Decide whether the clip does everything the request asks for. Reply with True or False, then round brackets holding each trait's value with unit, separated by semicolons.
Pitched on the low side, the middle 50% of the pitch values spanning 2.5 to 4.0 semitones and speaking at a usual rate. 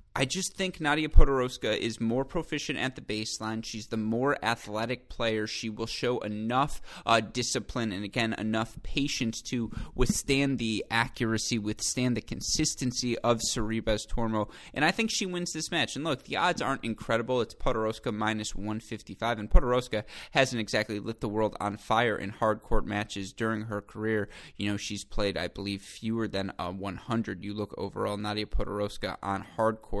True (110 Hz; 2.9 semitones; 175 wpm)